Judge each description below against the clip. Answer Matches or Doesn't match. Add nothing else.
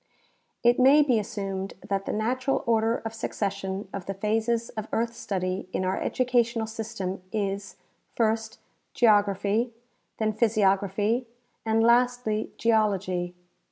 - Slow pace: Matches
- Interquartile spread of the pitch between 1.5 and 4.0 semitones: Matches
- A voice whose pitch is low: Doesn't match